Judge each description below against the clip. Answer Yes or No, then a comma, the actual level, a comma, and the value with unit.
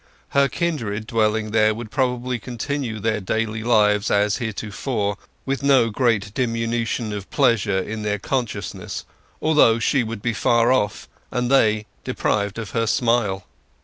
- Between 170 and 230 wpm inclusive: No, average, 145 wpm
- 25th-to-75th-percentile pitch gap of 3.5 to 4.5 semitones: No, narrow, 2.6 semitones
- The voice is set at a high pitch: No, low, 115 Hz